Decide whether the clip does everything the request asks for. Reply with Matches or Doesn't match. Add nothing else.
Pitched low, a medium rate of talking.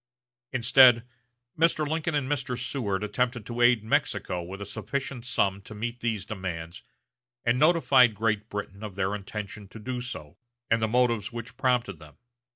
Matches